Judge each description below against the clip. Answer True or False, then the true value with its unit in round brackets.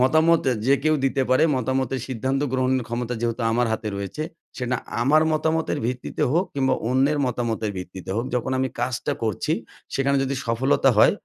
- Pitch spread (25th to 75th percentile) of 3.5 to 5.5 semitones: False (2.5 semitones)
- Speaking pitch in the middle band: False (130 Hz)